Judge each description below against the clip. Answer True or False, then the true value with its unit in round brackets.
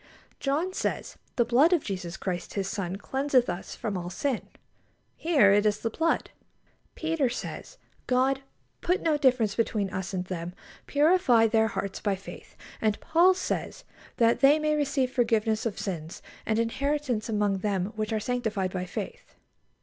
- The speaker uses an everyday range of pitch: False (6.1 semitones)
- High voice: True (225 Hz)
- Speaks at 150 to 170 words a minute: True (155 wpm)